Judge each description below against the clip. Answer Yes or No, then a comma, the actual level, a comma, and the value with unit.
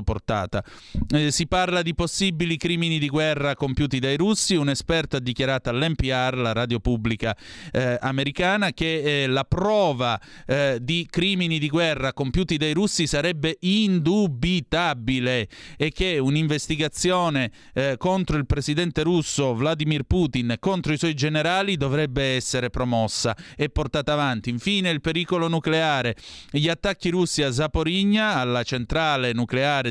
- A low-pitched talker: No, medium, 150 Hz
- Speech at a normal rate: Yes, average, 135 wpm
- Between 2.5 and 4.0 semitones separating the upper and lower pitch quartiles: No, average, 4.6 semitones